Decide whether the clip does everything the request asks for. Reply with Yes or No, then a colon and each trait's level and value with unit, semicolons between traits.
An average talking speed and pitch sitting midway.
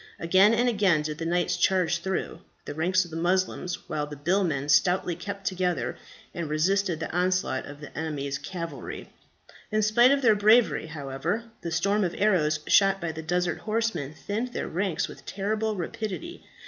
Yes: average, 175 wpm; medium, 180 Hz